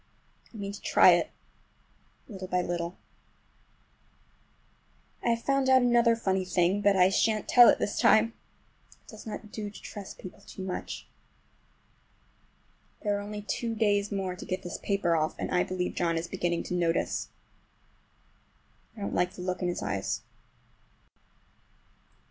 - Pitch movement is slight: No, average, 3.0 semitones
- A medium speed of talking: Yes, average, 155 wpm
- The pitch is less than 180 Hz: No, high, 195 Hz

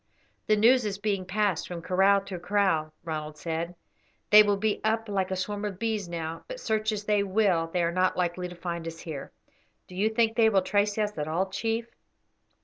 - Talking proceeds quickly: Yes, fast, 210 wpm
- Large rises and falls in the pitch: No, average, 3.5 semitones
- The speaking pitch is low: No, high, 195 Hz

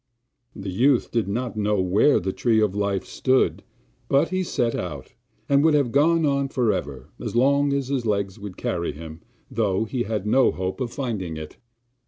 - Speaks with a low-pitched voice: Yes, low, 110 Hz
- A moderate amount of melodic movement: No, wide, 6.0 semitones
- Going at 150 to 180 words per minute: No, average, 190 wpm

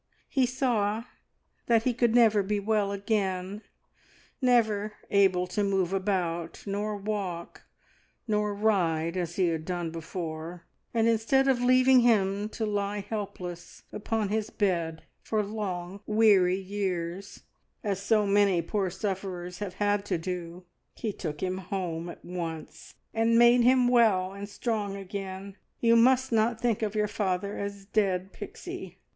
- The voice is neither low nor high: No, high, 200 Hz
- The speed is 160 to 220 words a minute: No, average, 145 wpm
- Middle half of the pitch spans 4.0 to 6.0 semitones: No, average, 3.2 semitones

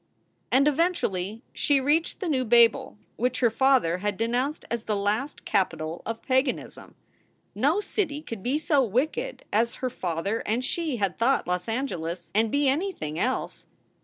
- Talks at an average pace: Yes, average, 160 wpm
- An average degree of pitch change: No, wide, 5.7 semitones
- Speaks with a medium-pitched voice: No, high, 240 Hz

